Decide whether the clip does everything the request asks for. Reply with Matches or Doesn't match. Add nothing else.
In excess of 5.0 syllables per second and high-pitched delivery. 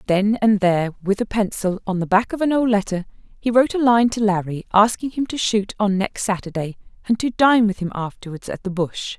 Matches